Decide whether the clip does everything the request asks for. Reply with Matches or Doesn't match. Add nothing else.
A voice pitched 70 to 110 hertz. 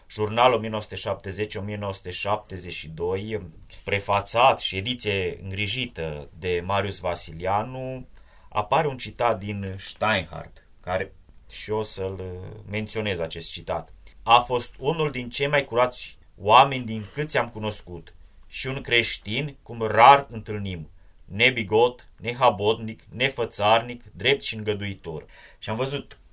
Matches